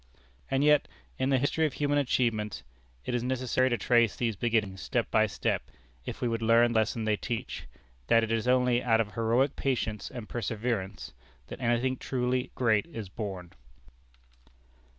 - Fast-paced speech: No, average, 170 wpm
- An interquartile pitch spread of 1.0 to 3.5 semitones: Yes, narrow, 2.6 semitones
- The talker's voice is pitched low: Yes, low, 120 Hz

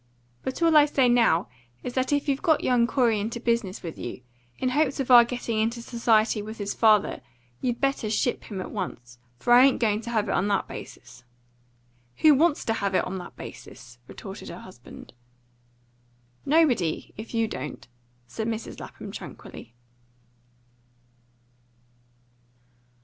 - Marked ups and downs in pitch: No, average, 4.1 semitones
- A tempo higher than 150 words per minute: Yes, average, 160 wpm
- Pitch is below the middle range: No, high, 230 Hz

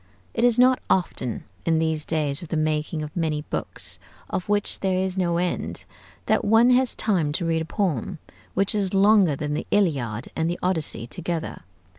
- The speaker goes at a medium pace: Yes, average, 185 wpm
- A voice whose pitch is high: No, medium, 170 Hz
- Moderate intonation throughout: Yes, average, 4.2 semitones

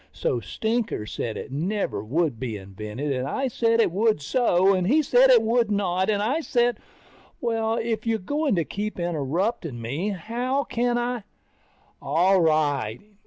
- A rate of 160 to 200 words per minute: Yes, average, 165 wpm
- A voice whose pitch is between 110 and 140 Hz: No, high, 205 Hz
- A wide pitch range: Yes, wide, 7.7 semitones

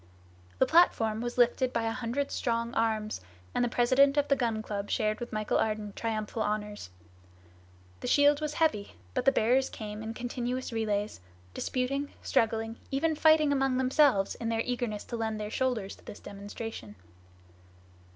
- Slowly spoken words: No, average, 160 wpm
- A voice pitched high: Yes, high, 230 Hz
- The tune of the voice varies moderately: Yes, average, 3.4 semitones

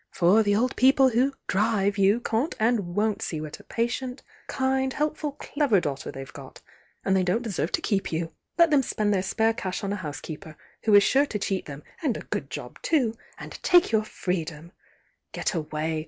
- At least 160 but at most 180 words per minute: No, average, 200 wpm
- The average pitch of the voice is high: Yes, high, 210 Hz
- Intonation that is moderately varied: No, wide, 6.2 semitones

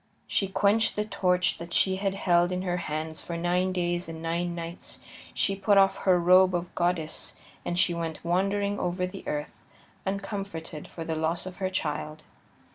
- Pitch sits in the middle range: Yes, medium, 180 Hz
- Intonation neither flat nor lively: No, narrow, 2.3 semitones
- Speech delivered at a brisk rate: No, average, 180 wpm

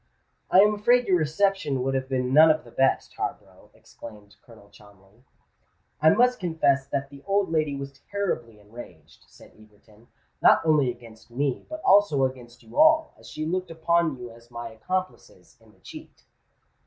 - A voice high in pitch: No, medium, 140 Hz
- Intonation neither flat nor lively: No, wide, 7.1 semitones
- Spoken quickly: No, average, 170 wpm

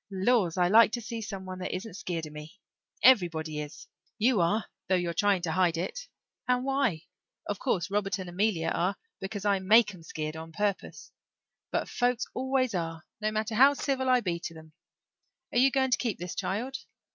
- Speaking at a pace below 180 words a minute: No, average, 195 wpm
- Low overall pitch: No, high, 195 Hz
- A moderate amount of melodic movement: No, wide, 5.7 semitones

